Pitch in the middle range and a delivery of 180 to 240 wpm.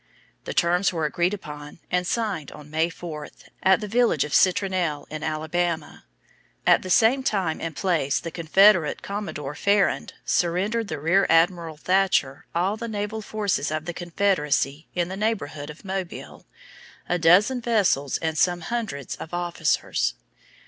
No: medium, 175 Hz; average, 150 wpm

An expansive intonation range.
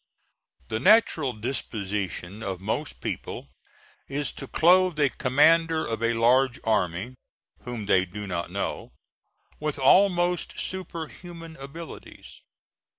Yes: wide, 7.1 semitones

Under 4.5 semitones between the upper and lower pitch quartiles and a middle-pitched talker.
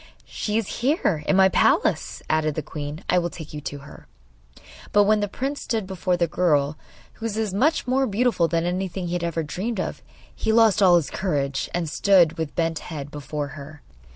No: average, 5.1 semitones; medium, 175 Hz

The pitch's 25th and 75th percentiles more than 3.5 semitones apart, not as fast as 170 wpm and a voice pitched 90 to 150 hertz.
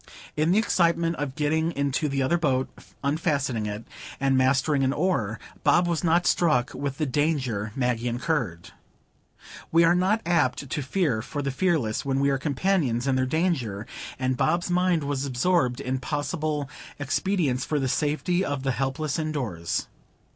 Yes: average, 4.2 semitones; average, 160 wpm; medium, 140 Hz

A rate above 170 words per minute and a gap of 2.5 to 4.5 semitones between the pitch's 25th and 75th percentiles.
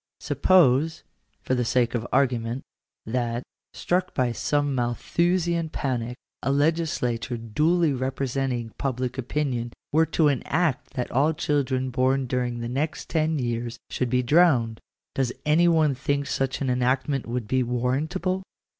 No: average, 145 wpm; average, 3.7 semitones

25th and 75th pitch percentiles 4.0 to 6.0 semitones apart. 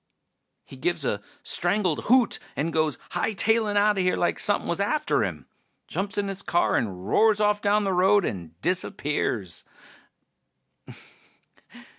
Yes: average, 5.1 semitones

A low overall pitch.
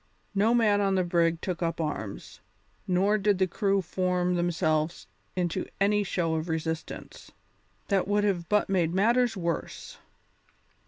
No: medium, 185 Hz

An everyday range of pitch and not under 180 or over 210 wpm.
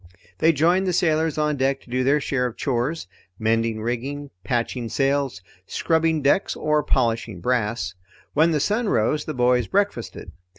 No: average, 4.6 semitones; average, 160 wpm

